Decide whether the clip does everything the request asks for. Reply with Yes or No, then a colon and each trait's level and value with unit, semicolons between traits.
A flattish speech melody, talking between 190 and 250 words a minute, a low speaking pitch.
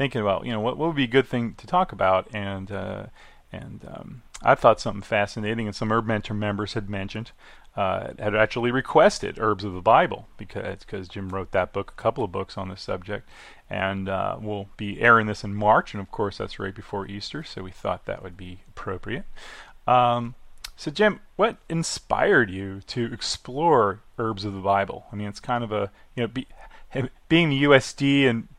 No: average, 3.8 semitones; average, 200 wpm; low, 110 Hz